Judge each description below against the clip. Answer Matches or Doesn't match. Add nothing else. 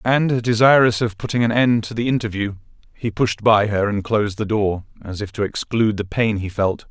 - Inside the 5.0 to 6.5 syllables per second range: Matches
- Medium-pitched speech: Doesn't match